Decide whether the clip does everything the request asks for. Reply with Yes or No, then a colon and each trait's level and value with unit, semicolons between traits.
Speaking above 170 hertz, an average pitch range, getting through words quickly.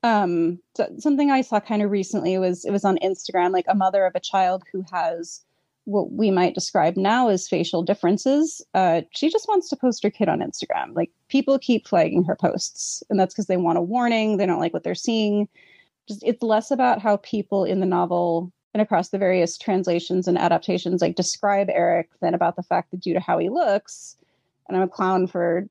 Yes: high, 190 Hz; average, 3.2 semitones; fast, 215 wpm